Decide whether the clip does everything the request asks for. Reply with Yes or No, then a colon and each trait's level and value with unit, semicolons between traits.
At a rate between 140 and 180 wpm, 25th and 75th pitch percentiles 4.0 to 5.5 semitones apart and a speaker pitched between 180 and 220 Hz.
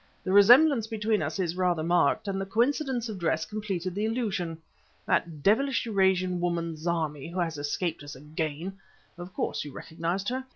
Yes: average, 170 wpm; average, 4.4 semitones; medium, 185 Hz